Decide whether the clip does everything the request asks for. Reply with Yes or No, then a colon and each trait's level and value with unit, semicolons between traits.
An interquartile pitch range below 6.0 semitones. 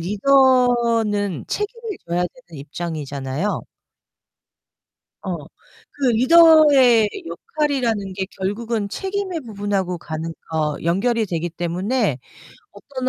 No: wide, 7.2 semitones